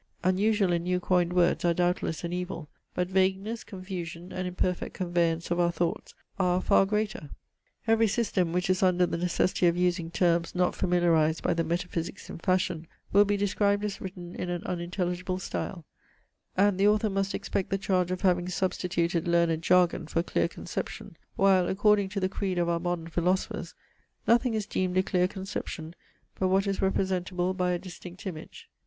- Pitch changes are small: Yes, narrow, 1.7 semitones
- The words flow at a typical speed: Yes, average, 180 wpm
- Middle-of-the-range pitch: Yes, medium, 180 Hz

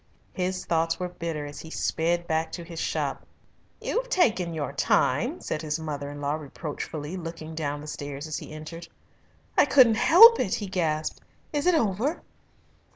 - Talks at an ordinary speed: Yes, average, 170 wpm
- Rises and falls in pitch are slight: No, average, 3.6 semitones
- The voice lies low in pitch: No, medium, 165 Hz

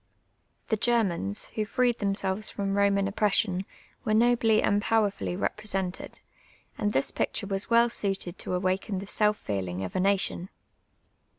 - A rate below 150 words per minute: Yes, average, 140 wpm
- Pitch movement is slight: Yes, narrow, 2.3 semitones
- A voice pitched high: Yes, high, 200 Hz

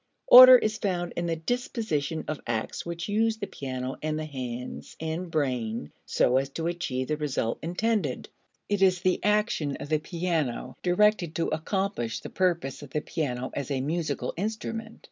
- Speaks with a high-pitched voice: No, medium, 165 Hz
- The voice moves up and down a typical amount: No, wide, 5.9 semitones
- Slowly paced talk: No, average, 170 wpm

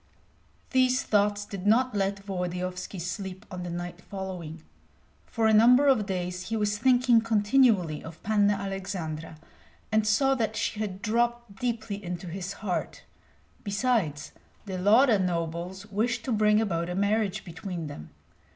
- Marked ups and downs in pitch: No, average, 3.6 semitones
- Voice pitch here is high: Yes, high, 200 Hz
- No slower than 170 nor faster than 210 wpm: No, average, 145 wpm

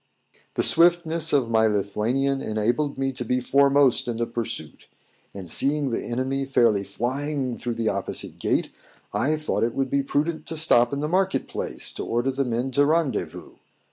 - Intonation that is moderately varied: Yes, average, 3.5 semitones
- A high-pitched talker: No, low, 135 Hz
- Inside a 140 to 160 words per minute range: No, average, 175 wpm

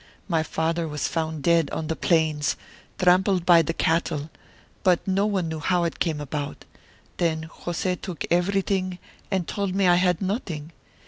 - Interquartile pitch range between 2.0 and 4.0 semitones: Yes, narrow, 2.6 semitones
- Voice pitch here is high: No, medium, 170 Hz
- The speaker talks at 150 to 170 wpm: Yes, average, 160 wpm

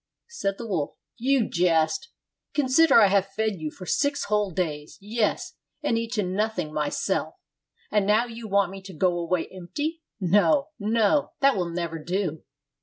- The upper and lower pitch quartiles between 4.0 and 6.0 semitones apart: Yes, average, 4.7 semitones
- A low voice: No, high, 200 Hz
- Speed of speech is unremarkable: Yes, average, 160 wpm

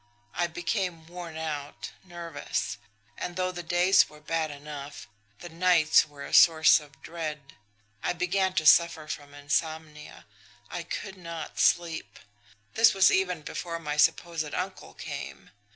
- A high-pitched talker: No, medium, 165 Hz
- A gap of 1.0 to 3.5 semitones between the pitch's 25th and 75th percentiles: Yes, narrow, 2.6 semitones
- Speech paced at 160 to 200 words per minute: No, average, 140 wpm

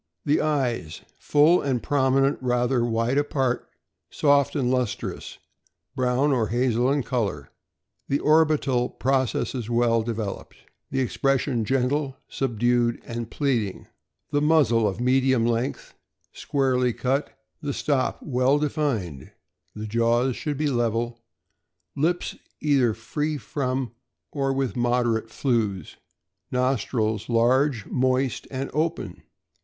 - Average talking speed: No, slow, 115 wpm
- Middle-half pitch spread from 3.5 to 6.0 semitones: No, average, 2.9 semitones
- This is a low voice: Yes, low, 125 Hz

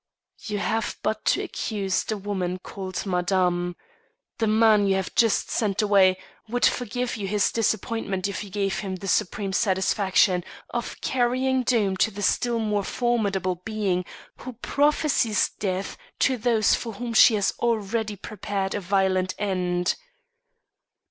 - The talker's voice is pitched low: No, high, 205 Hz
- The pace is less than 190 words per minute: Yes, average, 145 wpm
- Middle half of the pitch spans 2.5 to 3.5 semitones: Yes, average, 3.0 semitones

